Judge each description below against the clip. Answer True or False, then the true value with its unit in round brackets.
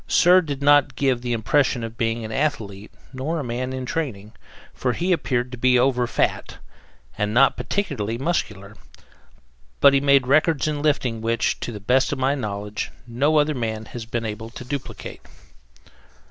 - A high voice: False (125 Hz)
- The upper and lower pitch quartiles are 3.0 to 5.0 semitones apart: True (4.0 semitones)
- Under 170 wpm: False (175 wpm)